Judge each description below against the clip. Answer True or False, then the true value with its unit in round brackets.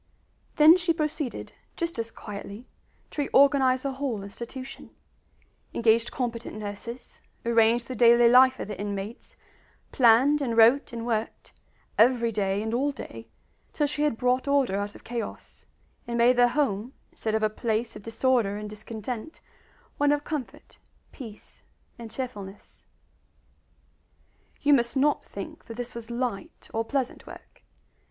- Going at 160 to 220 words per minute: False (145 wpm)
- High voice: True (235 Hz)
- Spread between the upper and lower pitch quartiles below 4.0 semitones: True (3.3 semitones)